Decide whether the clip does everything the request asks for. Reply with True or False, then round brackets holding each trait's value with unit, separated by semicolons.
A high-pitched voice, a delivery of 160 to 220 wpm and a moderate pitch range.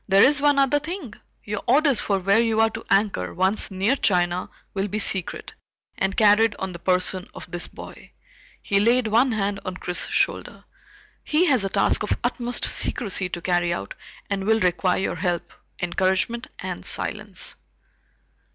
True (200 Hz; 170 wpm; 4.0 semitones)